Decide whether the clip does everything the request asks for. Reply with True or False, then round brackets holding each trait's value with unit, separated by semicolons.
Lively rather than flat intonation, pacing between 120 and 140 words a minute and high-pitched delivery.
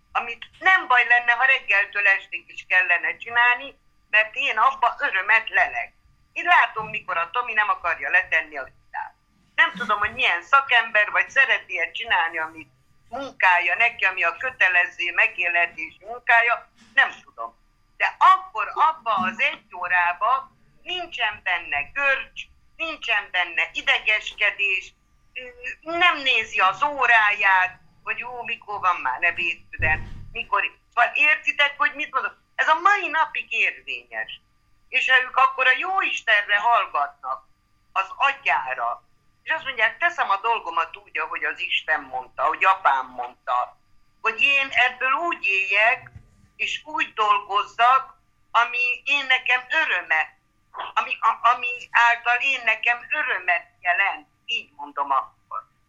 True (6.5 semitones; 135 wpm; 235 Hz)